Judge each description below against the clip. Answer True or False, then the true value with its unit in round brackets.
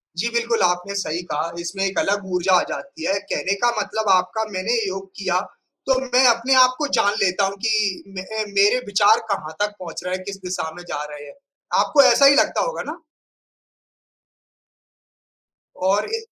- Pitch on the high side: True (200 Hz)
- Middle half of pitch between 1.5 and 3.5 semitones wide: False (4.1 semitones)